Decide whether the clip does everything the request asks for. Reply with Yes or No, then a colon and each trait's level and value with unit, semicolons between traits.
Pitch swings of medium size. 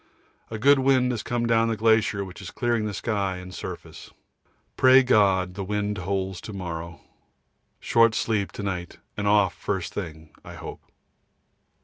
Yes: average, 3.5 semitones